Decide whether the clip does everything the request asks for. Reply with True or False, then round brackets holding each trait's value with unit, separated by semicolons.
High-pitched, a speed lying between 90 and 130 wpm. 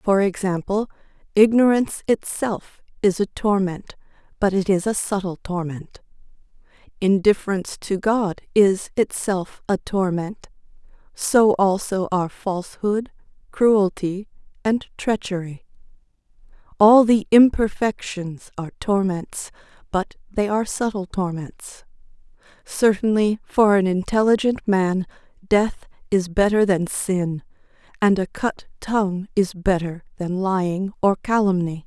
True (195 Hz; 105 wpm)